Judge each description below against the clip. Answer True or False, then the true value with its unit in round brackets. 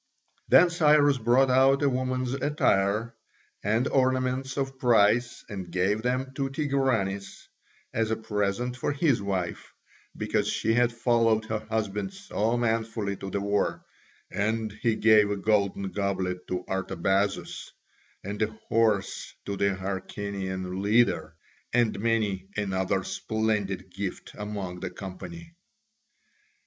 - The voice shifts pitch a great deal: False (4.1 semitones)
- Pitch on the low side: True (110 Hz)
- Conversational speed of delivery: False (125 wpm)